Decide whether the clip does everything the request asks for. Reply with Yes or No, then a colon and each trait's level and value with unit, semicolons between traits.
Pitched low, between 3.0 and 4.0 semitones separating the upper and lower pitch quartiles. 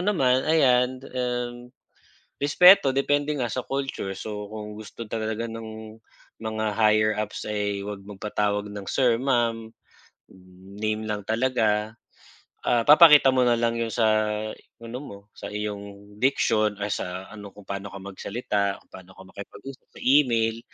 Yes: low, 110 Hz; average, 3.4 semitones